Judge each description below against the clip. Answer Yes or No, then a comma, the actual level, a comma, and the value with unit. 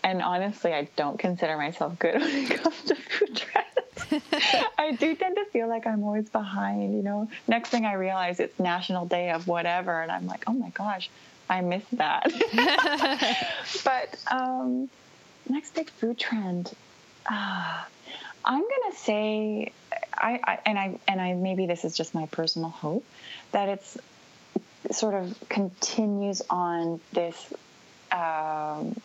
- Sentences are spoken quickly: No, average, 155 wpm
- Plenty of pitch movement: Yes, wide, 6.6 semitones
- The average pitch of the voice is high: Yes, high, 205 Hz